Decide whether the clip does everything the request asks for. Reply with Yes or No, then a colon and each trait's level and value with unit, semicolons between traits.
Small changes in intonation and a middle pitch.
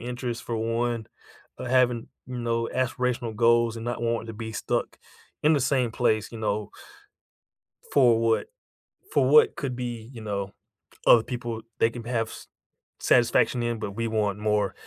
No: narrow, 1.7 semitones; low, 115 Hz